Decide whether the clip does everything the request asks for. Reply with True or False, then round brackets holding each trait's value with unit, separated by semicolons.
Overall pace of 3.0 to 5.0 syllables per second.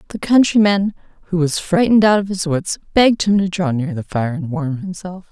False (5.5 syllables/s)